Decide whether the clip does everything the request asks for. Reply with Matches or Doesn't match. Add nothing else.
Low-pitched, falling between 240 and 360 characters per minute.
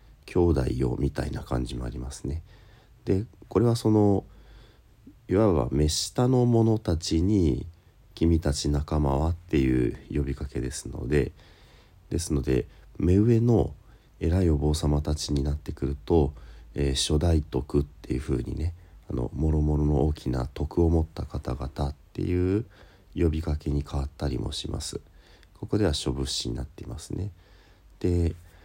Matches